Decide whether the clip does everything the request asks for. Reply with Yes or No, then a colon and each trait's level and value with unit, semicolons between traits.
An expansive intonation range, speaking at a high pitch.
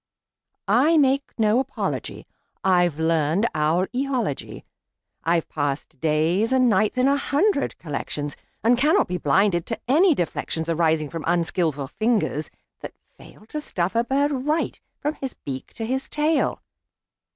Yes: wide, 8.6 semitones; high, 205 Hz